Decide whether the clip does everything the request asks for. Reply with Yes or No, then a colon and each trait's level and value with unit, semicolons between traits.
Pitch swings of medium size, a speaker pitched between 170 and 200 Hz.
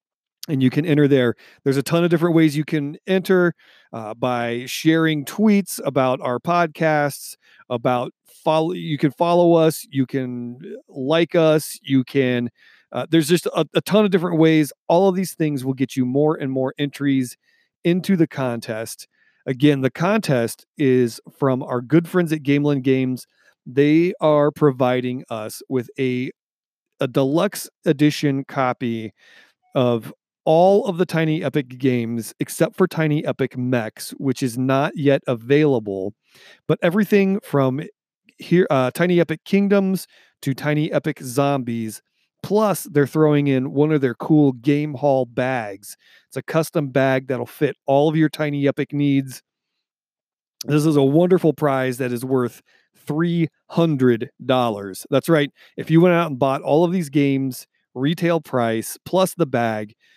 No: average, 4.0 semitones; medium, 145 Hz